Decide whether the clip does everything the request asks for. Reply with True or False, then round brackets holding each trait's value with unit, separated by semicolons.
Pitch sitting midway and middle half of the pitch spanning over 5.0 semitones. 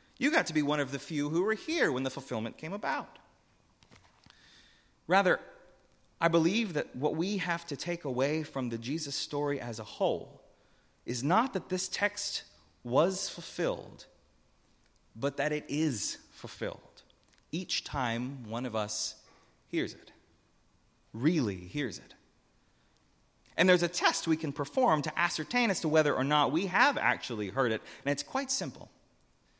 True (145 Hz; 5.5 semitones)